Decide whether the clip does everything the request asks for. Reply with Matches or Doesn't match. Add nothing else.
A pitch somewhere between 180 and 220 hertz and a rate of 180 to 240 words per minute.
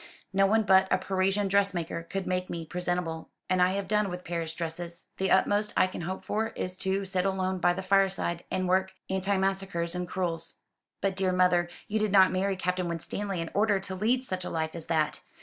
Matches